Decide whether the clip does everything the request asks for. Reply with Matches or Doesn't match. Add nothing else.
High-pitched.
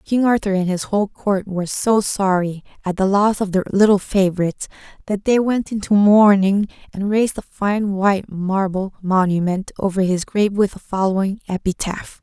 Matches